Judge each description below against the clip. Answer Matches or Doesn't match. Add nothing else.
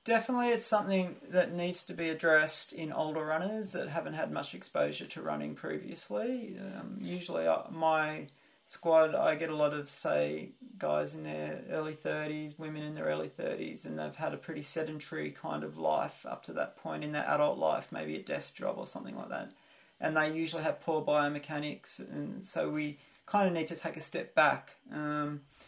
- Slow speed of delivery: Doesn't match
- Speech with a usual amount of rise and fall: Doesn't match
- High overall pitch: Doesn't match